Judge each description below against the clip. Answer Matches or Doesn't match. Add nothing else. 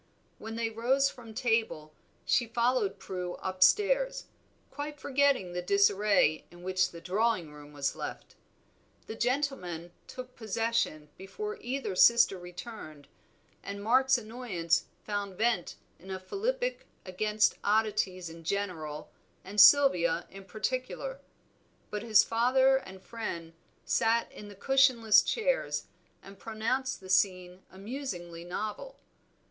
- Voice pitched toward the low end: Doesn't match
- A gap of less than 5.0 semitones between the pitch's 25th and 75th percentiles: Doesn't match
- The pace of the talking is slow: Matches